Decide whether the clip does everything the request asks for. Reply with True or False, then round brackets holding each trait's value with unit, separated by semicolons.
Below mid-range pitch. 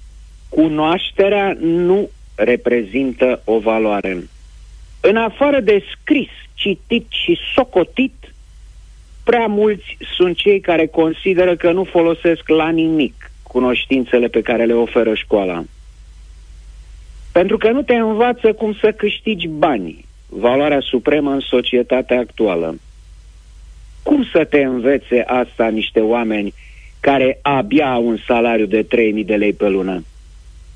True (125 Hz)